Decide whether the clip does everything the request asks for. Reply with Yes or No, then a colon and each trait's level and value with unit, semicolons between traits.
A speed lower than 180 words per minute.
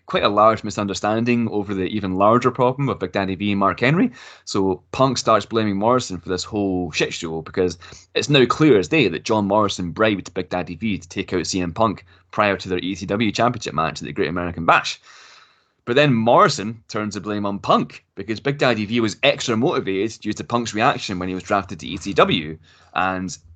No: fast, 205 wpm